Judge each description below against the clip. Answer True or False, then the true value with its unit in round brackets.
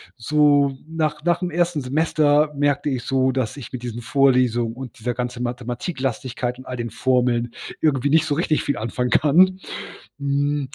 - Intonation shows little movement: False (3.3 semitones)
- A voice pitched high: False (135 Hz)